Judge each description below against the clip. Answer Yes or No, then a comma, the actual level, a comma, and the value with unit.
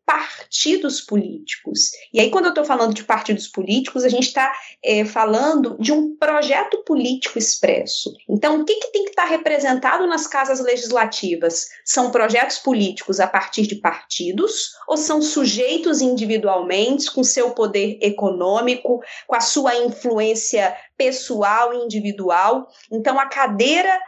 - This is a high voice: Yes, very high, 250 Hz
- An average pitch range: No, wide, 5.7 semitones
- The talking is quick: No, average, 145 wpm